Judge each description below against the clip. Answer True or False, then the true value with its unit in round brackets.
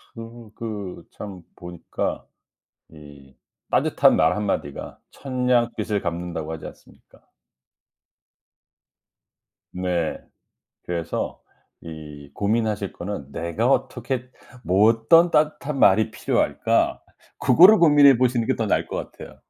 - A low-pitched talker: True (105 Hz)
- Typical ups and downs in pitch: False (6.2 semitones)